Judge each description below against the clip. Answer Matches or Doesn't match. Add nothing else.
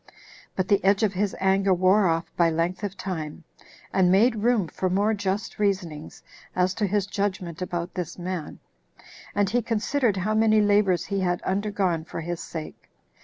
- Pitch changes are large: Doesn't match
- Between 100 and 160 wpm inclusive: Doesn't match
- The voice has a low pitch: Doesn't match